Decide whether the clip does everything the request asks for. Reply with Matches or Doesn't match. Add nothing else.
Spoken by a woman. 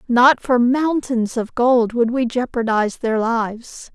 Matches